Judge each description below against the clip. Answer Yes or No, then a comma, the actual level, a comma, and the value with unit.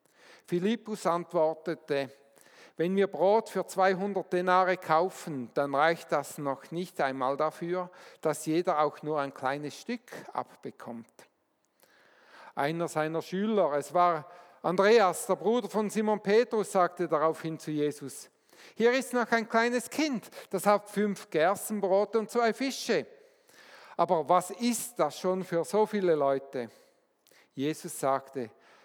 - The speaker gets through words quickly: No, average, 130 wpm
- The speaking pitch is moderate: Yes, medium, 175 Hz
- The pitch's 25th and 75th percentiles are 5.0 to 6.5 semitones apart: Yes, wide, 5.5 semitones